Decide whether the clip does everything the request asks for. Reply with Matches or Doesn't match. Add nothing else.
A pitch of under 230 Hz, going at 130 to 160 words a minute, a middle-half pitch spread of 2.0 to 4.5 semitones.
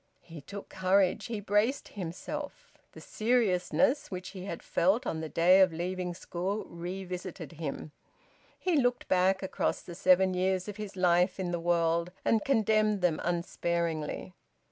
Matches